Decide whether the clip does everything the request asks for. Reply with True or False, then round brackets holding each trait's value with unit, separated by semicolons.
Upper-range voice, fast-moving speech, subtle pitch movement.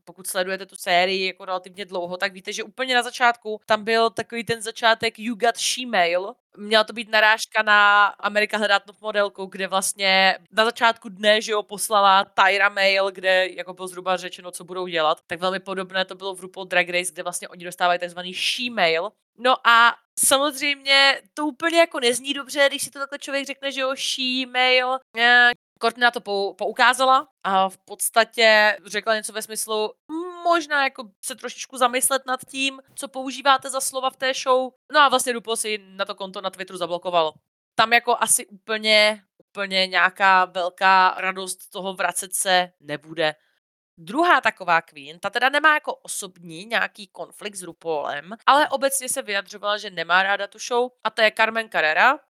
False (210 Hz; 180 wpm; 4.6 semitones)